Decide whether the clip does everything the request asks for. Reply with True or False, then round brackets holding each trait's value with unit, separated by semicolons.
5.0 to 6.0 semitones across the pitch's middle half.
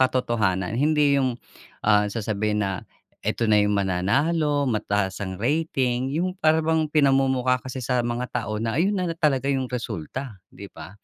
True (5.4 semitones)